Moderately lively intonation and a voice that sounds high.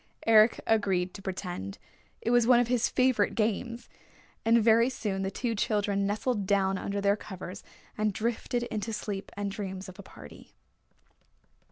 Yes: average, 3.0 semitones; high, 210 Hz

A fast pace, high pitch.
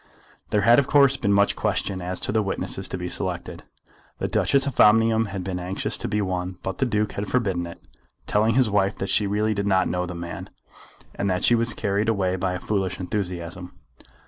No: fast, 215 wpm; low, 100 Hz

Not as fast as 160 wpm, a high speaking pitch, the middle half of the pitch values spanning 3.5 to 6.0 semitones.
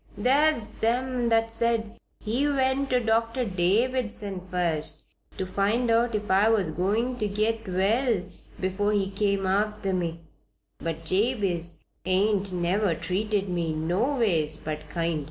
Yes: slow, 135 wpm; high, 205 Hz; average, 4.1 semitones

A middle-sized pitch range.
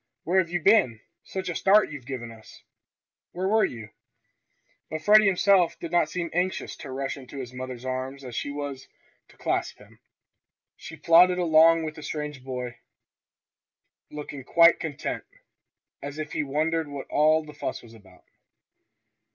Yes: average, 4.6 semitones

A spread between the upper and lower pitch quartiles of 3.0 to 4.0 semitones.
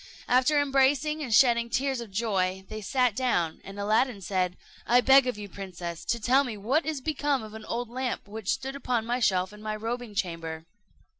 No: average, 4.6 semitones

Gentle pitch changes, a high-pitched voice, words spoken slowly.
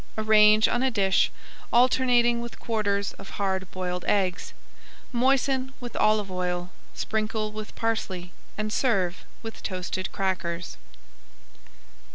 No: average, 3.9 semitones; high, 215 Hz; slow, 115 wpm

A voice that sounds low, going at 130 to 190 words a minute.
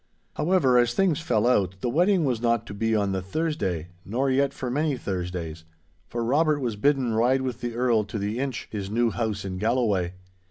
No: low, 120 Hz; average, 200 wpm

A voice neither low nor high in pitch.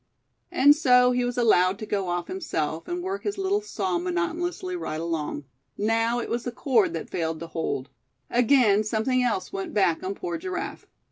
No: high, 240 Hz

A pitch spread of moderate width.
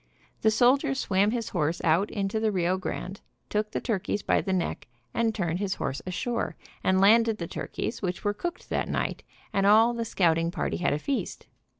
Yes: average, 3.9 semitones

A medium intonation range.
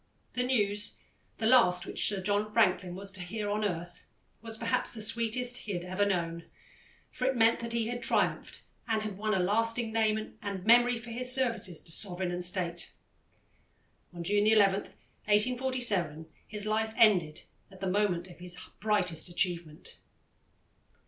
Yes: average, 4.1 semitones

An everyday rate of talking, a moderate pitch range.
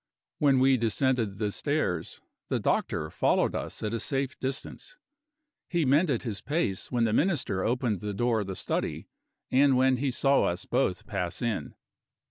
Yes: average, 165 wpm; average, 4.6 semitones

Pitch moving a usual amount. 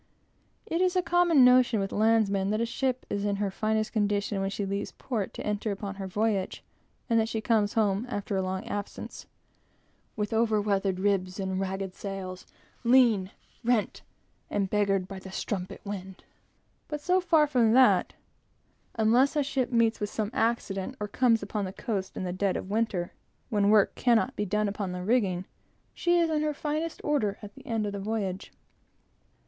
Yes: average, 3.3 semitones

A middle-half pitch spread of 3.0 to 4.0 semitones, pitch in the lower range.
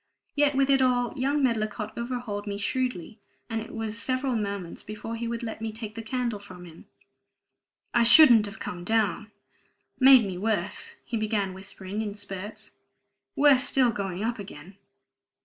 No: average, 3.3 semitones; high, 220 Hz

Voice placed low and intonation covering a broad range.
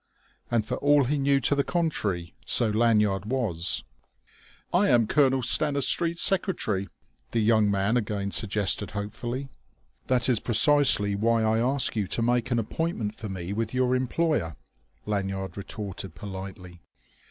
No: low, 115 Hz; average, 4.7 semitones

